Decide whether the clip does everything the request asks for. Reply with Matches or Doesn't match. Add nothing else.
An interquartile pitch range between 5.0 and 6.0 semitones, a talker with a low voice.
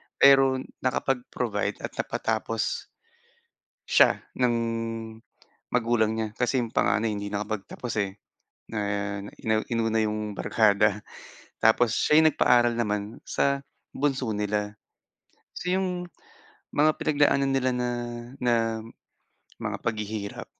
Doesn't match